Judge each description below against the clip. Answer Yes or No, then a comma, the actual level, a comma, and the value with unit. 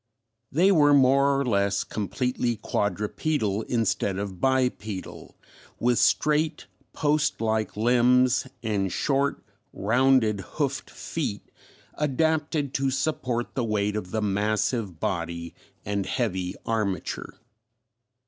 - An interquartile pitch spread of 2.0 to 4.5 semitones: No, average, 5.1 semitones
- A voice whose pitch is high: No, low, 120 Hz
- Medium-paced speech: No, slow, 105 wpm